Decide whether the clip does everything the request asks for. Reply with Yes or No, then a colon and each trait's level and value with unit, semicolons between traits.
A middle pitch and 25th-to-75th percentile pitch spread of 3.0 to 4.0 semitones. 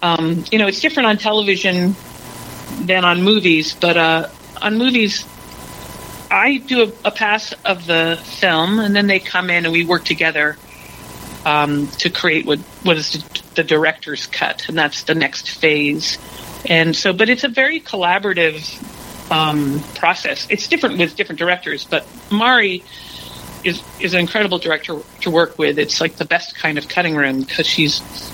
No: medium, 170 Hz; average, 4.5 semitones